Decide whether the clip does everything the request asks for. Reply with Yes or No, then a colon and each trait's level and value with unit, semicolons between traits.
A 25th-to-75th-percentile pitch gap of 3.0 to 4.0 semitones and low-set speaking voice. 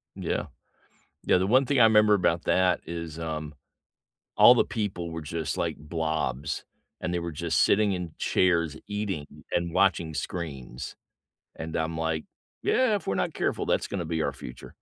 Yes: average, 3.3 semitones; very low, 85 Hz